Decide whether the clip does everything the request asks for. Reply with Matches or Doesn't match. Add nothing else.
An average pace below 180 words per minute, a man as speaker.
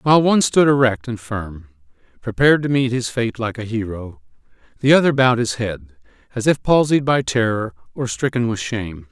Doesn't match